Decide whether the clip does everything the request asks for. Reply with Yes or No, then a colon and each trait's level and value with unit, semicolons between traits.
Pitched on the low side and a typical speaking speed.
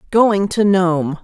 No: high, 190 Hz; average, 145 wpm